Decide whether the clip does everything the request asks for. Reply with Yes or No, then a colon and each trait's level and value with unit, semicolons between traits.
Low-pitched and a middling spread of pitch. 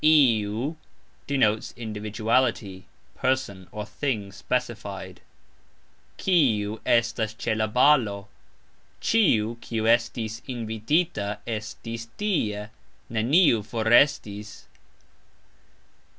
Yes: low, 110 Hz; average, 3.4 semitones